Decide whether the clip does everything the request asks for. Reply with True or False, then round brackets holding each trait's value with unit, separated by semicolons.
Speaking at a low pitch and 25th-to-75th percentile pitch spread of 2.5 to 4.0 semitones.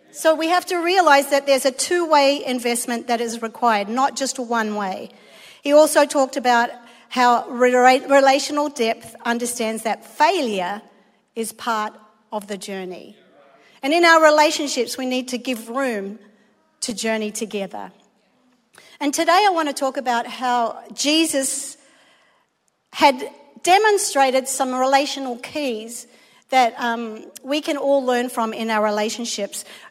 False (255 Hz; 3.5 semitones)